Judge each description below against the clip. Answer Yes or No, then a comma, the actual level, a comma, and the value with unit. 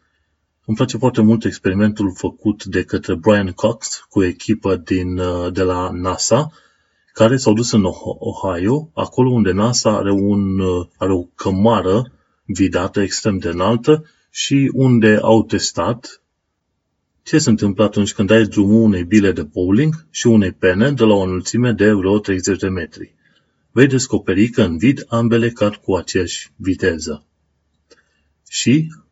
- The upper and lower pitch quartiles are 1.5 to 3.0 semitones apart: No, average, 3.5 semitones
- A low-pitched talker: Yes, low, 105 Hz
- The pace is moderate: Yes, average, 145 wpm